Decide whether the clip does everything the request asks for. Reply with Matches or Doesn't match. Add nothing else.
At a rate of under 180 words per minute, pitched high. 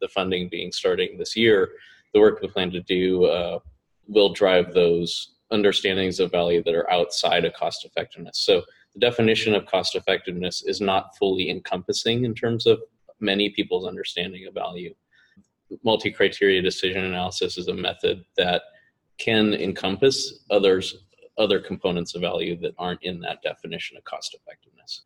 Doesn't match